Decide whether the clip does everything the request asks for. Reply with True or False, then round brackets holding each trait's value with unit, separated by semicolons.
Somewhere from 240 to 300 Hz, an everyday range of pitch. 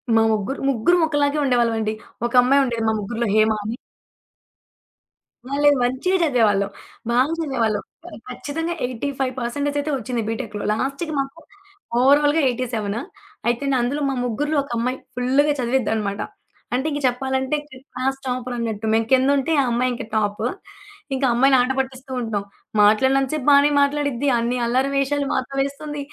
True (255 Hz; 3.2 semitones)